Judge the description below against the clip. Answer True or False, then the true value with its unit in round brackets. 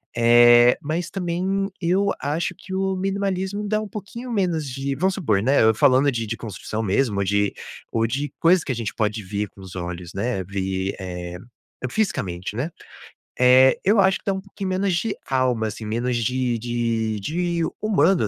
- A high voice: False (130 Hz)